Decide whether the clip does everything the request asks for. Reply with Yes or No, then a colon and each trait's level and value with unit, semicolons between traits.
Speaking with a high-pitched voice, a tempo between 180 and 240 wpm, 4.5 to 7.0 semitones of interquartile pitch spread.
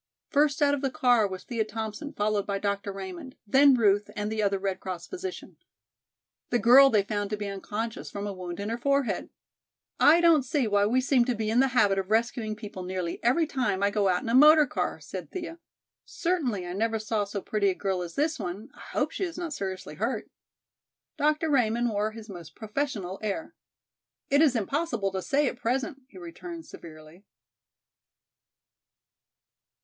Yes: high, 220 Hz; average, 190 wpm; wide, 5.5 semitones